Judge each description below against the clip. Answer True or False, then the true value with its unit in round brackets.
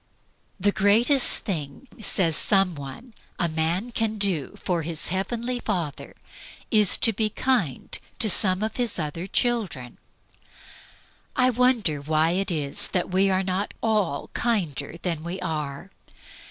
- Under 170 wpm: True (140 wpm)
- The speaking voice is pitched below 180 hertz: False (190 Hz)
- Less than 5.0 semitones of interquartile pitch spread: False (5.4 semitones)